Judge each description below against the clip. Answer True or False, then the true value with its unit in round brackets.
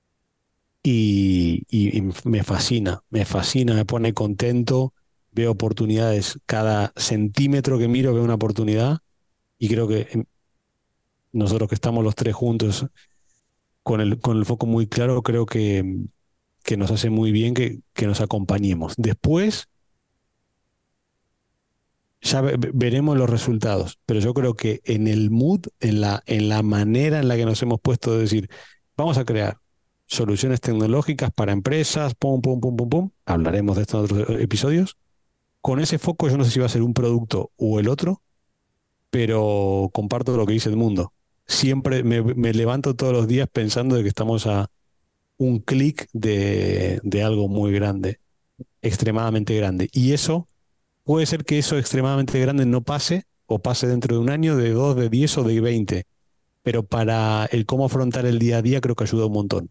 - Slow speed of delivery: False (170 wpm)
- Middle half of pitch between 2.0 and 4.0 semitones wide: True (3.3 semitones)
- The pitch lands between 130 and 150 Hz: False (115 Hz)